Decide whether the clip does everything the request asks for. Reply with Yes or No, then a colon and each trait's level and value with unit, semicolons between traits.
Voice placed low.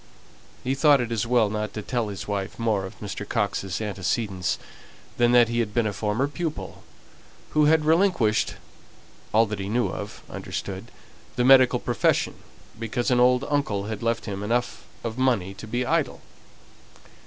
Yes: low, 115 Hz